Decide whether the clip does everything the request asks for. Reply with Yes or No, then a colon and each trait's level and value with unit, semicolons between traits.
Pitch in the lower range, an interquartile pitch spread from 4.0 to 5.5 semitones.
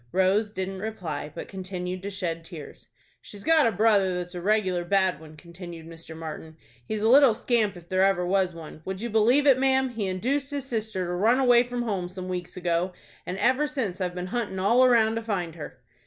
No: high, 190 Hz; average, 4.3 semitones